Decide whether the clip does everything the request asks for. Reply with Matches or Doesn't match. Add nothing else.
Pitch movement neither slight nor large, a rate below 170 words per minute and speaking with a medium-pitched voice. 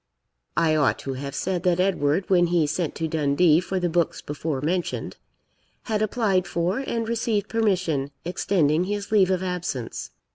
Matches